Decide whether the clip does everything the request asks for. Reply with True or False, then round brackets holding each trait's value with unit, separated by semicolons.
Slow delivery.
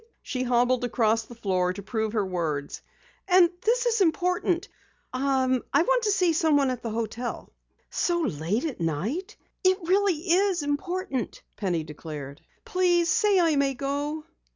False (150 wpm)